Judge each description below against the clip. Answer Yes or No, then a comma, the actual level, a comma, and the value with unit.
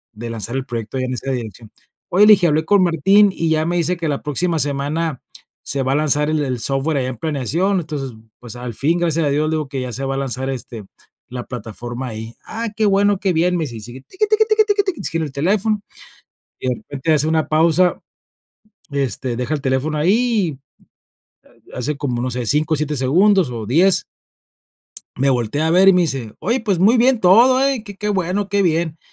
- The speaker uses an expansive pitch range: Yes, wide, 6.1 semitones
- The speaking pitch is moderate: Yes, medium, 155 Hz